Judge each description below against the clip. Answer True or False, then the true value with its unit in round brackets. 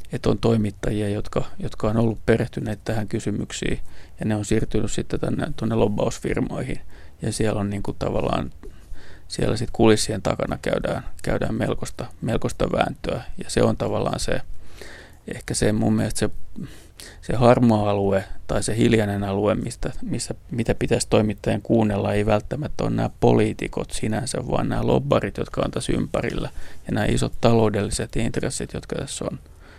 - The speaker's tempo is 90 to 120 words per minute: False (155 wpm)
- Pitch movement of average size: False (1.9 semitones)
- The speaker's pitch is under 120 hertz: True (105 Hz)